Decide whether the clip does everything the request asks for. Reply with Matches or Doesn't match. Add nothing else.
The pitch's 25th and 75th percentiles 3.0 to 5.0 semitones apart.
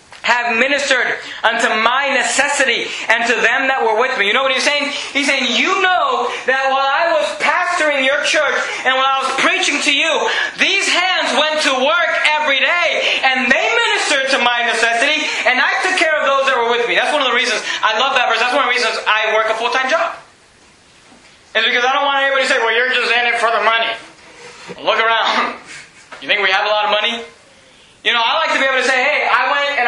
Matches